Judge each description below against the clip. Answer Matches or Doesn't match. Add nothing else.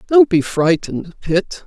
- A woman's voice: Matches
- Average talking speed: Matches